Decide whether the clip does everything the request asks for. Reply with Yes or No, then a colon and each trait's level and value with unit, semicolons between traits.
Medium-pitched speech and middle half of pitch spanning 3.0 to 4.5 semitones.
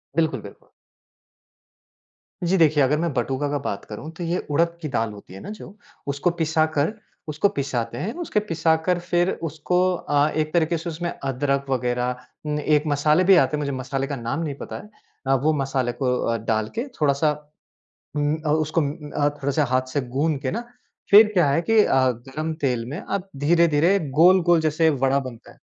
Yes: medium, 150 Hz; average, 3.7 semitones